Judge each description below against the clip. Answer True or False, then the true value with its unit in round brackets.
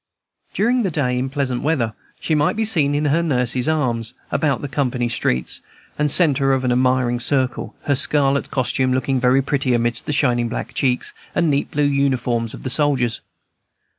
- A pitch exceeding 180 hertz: False (135 Hz)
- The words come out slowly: False (180 wpm)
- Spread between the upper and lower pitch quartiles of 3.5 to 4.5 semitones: False (2.8 semitones)